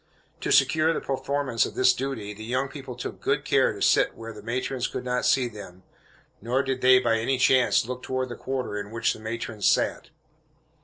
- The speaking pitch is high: No, low, 125 Hz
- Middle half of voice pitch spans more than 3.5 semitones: No, narrow, 2.6 semitones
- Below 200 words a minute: No, fast, 205 wpm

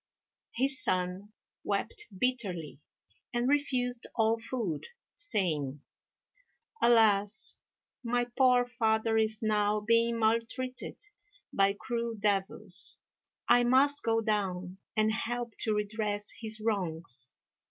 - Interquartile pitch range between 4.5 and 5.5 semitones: No, average, 3.1 semitones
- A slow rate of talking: Yes, slow, 100 wpm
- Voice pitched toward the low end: No, high, 220 Hz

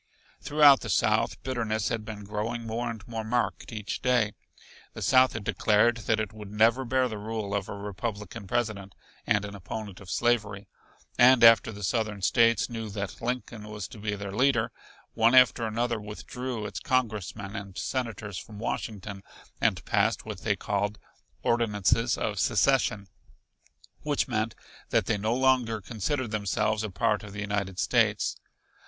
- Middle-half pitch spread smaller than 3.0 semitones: Yes, narrow, 2.5 semitones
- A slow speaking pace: No, average, 160 wpm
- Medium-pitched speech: No, low, 110 Hz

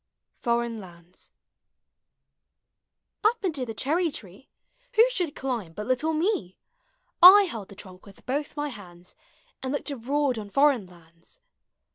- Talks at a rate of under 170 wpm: Yes, slow, 135 wpm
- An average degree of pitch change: No, wide, 7.3 semitones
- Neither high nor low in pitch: No, very high, 250 Hz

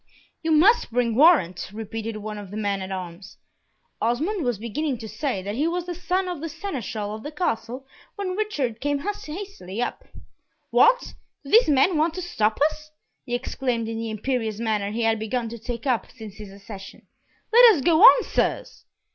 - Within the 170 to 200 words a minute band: Yes, average, 190 wpm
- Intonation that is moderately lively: No, wide, 7.1 semitones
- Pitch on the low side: No, high, 245 Hz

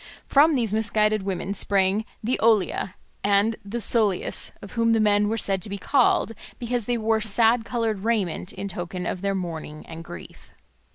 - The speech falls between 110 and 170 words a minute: No, average, 180 wpm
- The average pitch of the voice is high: Yes, high, 210 Hz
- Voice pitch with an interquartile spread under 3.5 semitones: Yes, average, 2.9 semitones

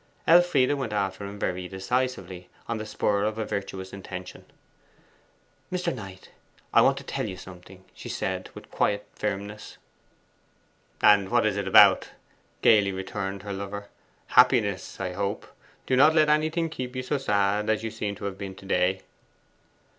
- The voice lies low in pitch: Yes, low, 100 Hz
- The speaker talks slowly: No, average, 160 wpm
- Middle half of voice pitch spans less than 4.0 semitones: Yes, average, 3.6 semitones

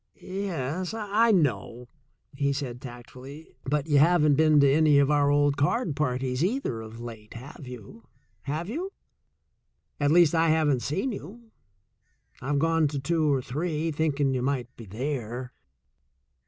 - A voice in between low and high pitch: Yes, medium, 145 Hz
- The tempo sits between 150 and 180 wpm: No, average, 140 wpm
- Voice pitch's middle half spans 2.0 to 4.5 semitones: Yes, average, 4.0 semitones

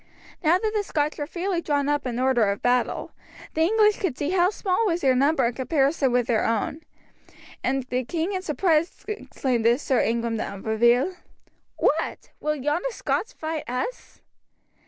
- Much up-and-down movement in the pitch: Yes, wide, 5.9 semitones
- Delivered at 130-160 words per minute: No, average, 175 wpm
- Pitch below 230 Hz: No, very high, 290 Hz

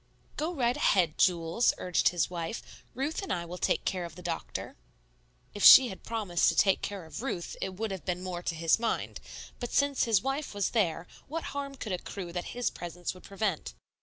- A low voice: No, high, 190 Hz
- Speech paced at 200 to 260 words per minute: Yes, fast, 205 wpm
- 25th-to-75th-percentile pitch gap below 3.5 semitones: No, wide, 5.6 semitones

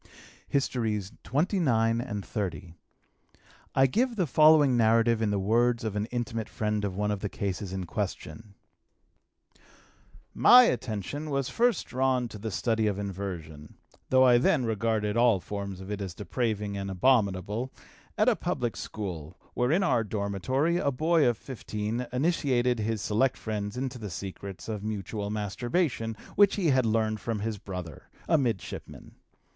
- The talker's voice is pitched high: No, low, 110 Hz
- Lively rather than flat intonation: No, average, 4.0 semitones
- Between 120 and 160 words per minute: Yes, average, 155 wpm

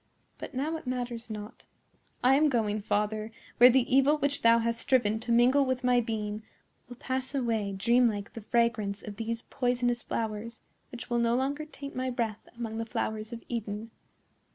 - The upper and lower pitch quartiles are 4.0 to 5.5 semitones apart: No, narrow, 2.6 semitones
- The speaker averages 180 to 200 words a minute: Yes, average, 190 wpm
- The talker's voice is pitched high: Yes, high, 235 Hz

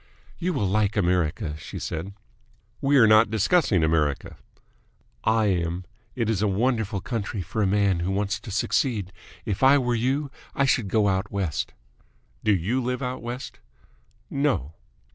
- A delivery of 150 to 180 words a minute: Yes, average, 160 wpm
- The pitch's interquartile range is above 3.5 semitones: Yes, average, 4.7 semitones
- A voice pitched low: Yes, low, 105 Hz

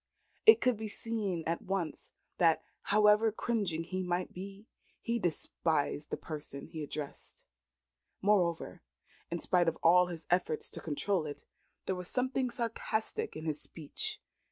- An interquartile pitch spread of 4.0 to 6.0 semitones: Yes, average, 4.6 semitones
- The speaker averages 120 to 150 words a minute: Yes, average, 145 wpm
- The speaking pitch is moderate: Yes, medium, 180 Hz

